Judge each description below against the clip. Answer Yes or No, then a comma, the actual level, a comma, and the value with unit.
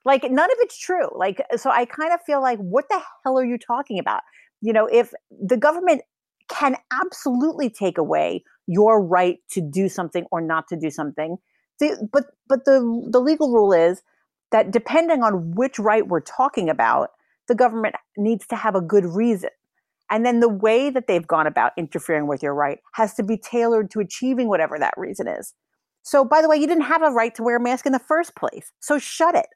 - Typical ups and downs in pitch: No, wide, 6.3 semitones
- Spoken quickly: Yes, fast, 210 wpm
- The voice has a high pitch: Yes, high, 235 Hz